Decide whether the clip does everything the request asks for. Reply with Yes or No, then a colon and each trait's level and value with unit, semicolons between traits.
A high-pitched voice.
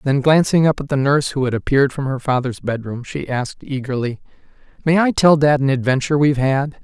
No: low, 135 Hz